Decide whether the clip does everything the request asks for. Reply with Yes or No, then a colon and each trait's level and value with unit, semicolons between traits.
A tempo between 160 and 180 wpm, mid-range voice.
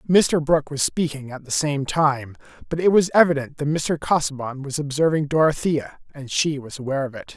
No: average, 195 wpm; medium, 145 Hz